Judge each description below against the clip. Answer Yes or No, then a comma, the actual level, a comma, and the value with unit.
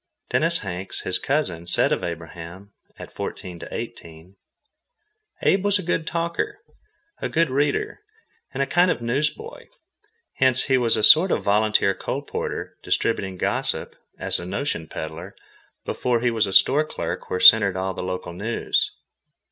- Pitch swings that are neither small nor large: No, wide, 8.4 semitones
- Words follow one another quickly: No, average, 155 wpm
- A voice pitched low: Yes, low, 110 Hz